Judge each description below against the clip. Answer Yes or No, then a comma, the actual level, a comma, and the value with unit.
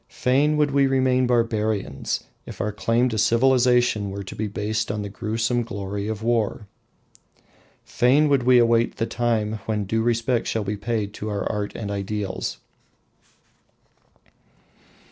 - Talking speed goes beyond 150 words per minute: No, average, 145 wpm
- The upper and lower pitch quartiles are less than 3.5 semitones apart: Yes, average, 2.8 semitones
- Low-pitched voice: Yes, low, 115 Hz